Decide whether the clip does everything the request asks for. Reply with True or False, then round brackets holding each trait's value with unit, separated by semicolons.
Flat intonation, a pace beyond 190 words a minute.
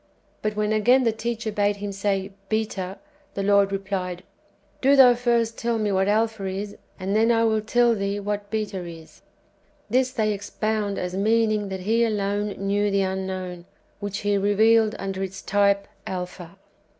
False (2.1 semitones; 175 wpm)